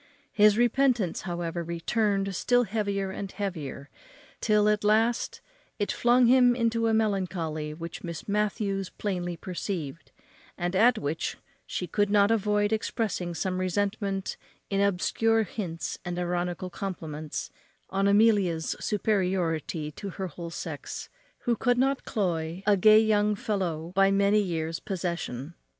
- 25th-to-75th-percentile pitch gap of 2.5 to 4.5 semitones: Yes, average, 3.5 semitones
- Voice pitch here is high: Yes, high, 195 Hz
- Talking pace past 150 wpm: No, slow, 135 wpm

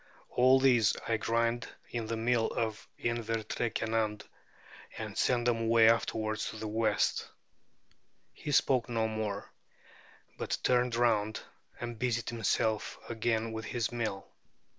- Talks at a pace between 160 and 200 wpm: No, slow, 135 wpm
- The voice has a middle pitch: No, low, 115 Hz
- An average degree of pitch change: No, narrow, 1.4 semitones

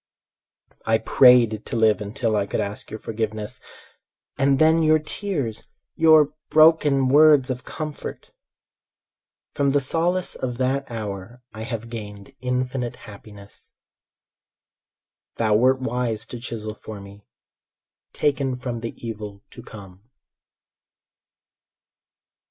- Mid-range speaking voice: No, low, 120 Hz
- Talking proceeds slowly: Yes, slow, 115 wpm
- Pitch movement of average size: Yes, average, 4.2 semitones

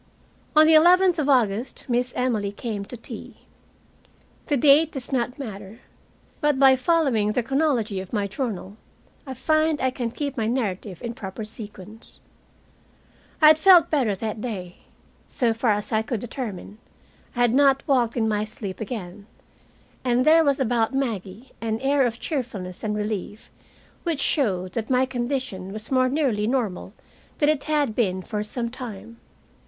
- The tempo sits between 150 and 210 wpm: Yes, average, 160 wpm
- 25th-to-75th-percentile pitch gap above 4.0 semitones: Yes, average, 4.4 semitones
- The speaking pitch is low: No, high, 240 Hz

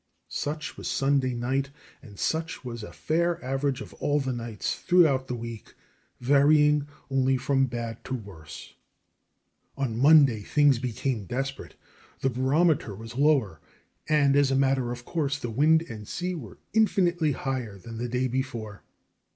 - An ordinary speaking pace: Yes, average, 150 wpm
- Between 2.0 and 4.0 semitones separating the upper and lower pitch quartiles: Yes, average, 3.6 semitones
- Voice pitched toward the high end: No, low, 135 Hz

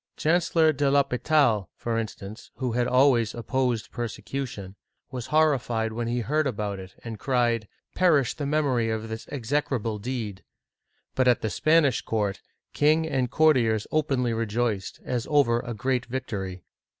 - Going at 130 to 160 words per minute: Yes, average, 150 wpm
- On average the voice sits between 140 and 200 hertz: No, low, 120 Hz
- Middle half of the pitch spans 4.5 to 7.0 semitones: No, average, 3.8 semitones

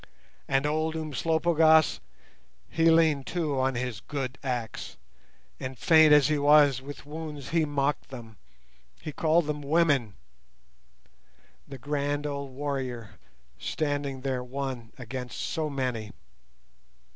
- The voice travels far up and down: No, average, 3.1 semitones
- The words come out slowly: Yes, slow, 115 wpm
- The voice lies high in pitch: No, medium, 140 Hz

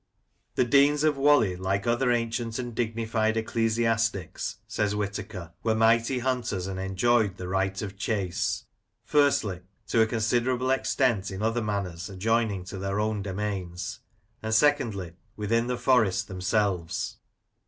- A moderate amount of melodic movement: Yes, average, 3.6 semitones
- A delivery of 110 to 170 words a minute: Yes, average, 145 wpm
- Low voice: Yes, low, 110 Hz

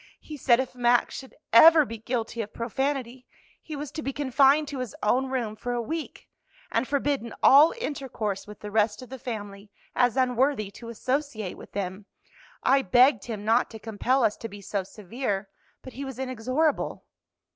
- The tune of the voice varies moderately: Yes, average, 3.8 semitones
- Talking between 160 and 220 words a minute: Yes, average, 180 wpm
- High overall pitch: Yes, high, 245 Hz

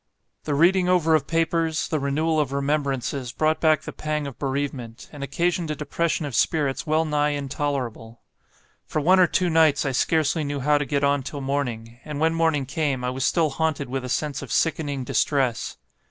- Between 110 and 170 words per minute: No, average, 195 wpm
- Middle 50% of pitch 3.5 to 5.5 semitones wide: No, average, 2.7 semitones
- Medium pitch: Yes, medium, 145 Hz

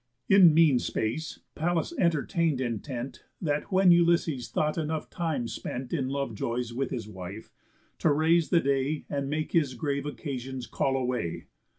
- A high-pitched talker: No, medium, 140 Hz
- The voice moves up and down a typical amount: Yes, average, 4.5 semitones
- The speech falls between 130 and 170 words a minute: Yes, average, 155 wpm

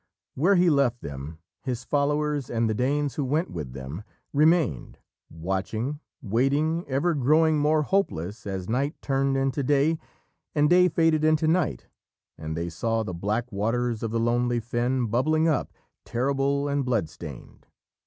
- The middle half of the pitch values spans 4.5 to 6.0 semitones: Yes, average, 5.2 semitones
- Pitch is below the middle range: Yes, low, 130 Hz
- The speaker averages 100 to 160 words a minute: Yes, average, 155 wpm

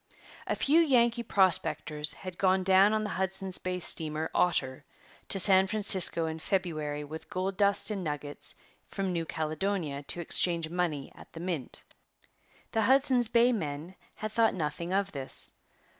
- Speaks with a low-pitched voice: No, medium, 185 Hz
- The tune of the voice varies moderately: Yes, average, 4.2 semitones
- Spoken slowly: No, average, 160 wpm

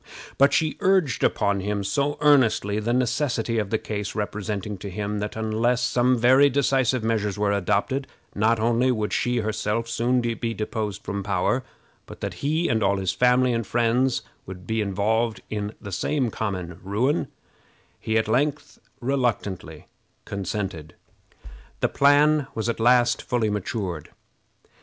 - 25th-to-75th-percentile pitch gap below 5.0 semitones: Yes, average, 3.5 semitones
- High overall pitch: No, low, 110 Hz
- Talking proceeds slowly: No, average, 150 wpm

